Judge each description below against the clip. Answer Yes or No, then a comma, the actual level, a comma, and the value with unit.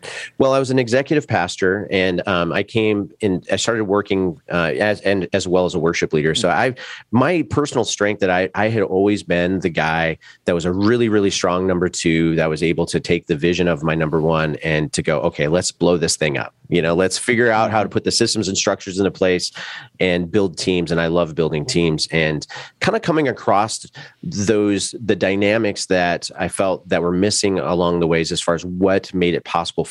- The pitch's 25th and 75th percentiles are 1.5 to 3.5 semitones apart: Yes, average, 3.2 semitones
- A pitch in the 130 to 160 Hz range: No, very low, 95 Hz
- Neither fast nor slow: No, fast, 225 wpm